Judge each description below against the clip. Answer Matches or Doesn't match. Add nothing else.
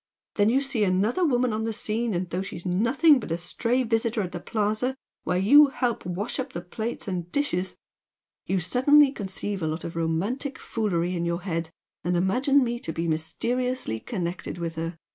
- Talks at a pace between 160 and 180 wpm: Doesn't match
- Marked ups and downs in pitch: Matches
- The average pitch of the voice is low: Doesn't match